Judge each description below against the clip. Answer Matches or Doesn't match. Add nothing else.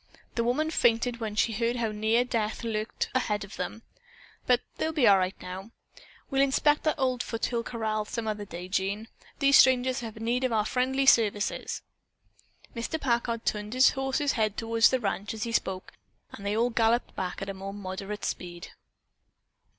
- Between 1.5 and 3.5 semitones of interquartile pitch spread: Matches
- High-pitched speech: Matches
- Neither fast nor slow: Matches